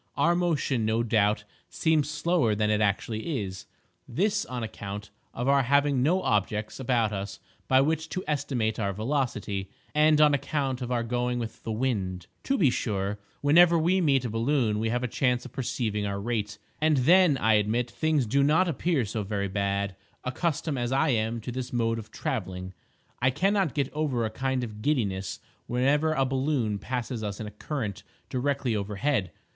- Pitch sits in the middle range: No, low, 125 Hz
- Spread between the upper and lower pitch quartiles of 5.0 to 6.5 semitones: Yes, average, 5.3 semitones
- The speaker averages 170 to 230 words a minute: Yes, average, 180 wpm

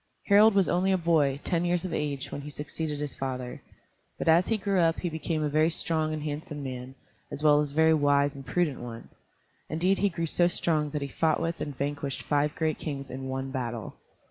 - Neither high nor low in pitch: Yes, medium, 150 Hz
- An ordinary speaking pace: No, fast, 220 wpm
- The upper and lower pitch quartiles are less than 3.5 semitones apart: Yes, average, 3.0 semitones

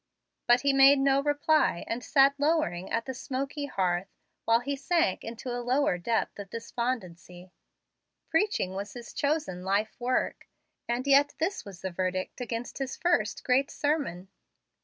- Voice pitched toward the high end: Yes, high, 245 Hz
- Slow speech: No, average, 155 wpm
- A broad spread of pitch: Yes, wide, 6.2 semitones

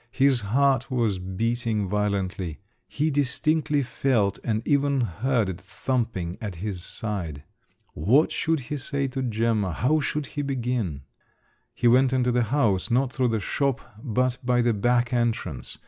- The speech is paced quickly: No, average, 150 wpm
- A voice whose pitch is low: Yes, low, 120 Hz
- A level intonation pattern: No, average, 4.6 semitones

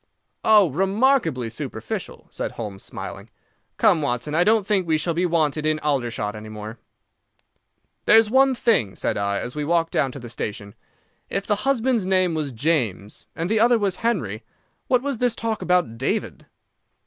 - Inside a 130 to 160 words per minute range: No, average, 170 wpm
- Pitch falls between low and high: Yes, medium, 165 Hz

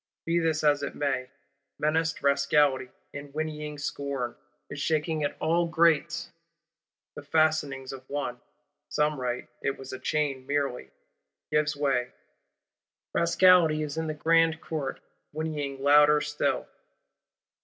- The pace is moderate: No, slow, 125 wpm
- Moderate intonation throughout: No, narrow, 2.1 semitones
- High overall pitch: No, medium, 150 Hz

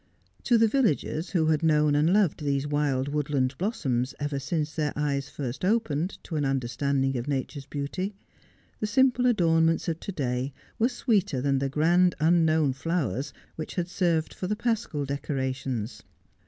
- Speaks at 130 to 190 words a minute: Yes, average, 160 wpm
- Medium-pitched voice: Yes, medium, 150 Hz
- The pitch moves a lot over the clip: No, average, 4.5 semitones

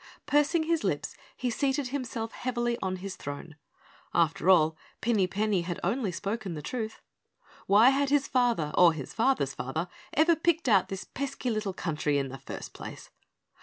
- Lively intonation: Yes, wide, 7.3 semitones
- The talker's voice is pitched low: No, high, 215 Hz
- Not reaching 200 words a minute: Yes, average, 165 wpm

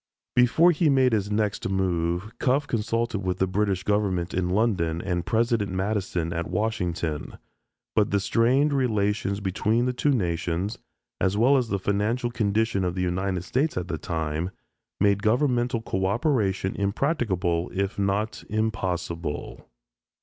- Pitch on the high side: No, low, 100 Hz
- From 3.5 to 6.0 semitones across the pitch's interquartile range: Yes, average, 4.1 semitones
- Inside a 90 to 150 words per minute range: Yes, average, 140 wpm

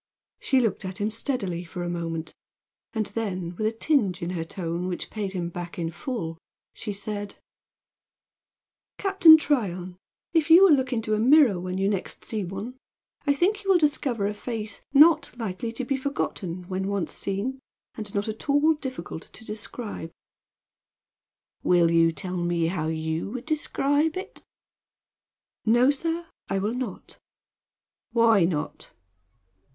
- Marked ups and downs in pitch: Yes, wide, 6.7 semitones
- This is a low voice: No, high, 210 Hz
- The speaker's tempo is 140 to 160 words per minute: Yes, average, 155 wpm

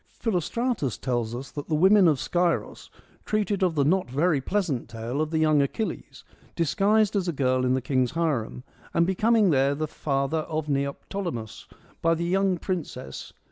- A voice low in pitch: No, medium, 155 Hz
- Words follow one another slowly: No, average, 170 wpm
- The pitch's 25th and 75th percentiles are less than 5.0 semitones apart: No, wide, 5.5 semitones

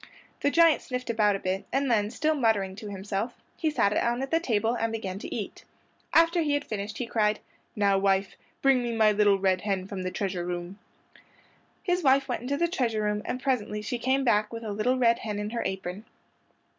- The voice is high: Yes, high, 220 Hz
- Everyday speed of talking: No, fast, 215 wpm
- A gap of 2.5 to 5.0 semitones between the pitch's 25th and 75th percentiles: Yes, average, 4.2 semitones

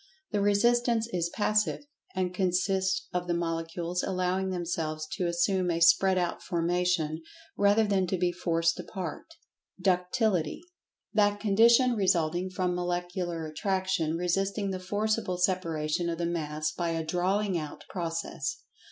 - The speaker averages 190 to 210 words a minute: No, slow, 135 wpm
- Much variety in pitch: No, narrow, 2.5 semitones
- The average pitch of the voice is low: No, medium, 180 Hz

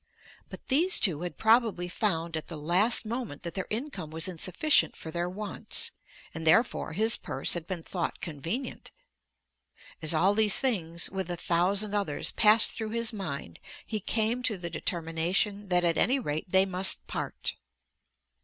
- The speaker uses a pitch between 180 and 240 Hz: Yes, high, 190 Hz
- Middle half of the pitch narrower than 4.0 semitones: No, average, 4.7 semitones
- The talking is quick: No, average, 165 wpm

